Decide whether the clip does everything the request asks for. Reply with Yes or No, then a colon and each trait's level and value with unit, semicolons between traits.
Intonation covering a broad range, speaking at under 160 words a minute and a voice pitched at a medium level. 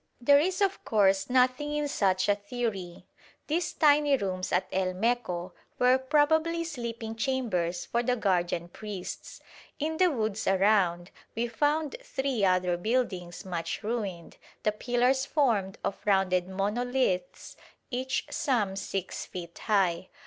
No: wide, 5.8 semitones; slow, 135 wpm; high, 220 Hz